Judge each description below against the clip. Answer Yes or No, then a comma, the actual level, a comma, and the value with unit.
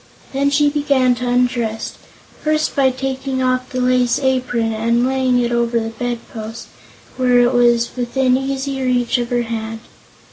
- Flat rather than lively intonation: Yes, narrow, 1.8 semitones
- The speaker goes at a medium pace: Yes, average, 150 wpm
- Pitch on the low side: No, very high, 250 Hz